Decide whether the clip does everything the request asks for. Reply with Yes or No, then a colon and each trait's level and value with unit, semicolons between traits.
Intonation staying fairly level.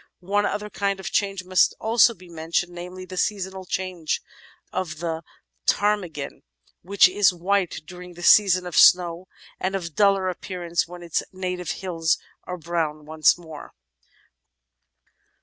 Yes: narrow, 2.1 semitones